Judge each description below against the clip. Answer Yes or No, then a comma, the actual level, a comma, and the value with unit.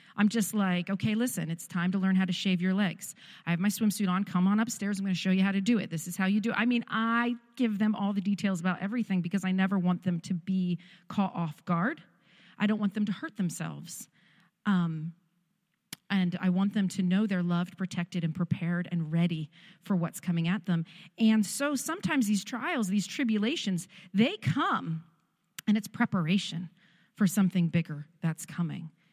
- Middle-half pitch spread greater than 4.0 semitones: No, average, 2.9 semitones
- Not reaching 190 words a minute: No, fast, 205 wpm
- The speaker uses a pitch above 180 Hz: Yes, high, 190 Hz